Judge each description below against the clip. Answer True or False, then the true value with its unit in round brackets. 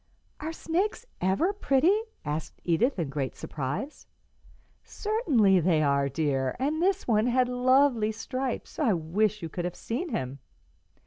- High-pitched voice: True (220 Hz)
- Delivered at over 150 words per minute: False (140 wpm)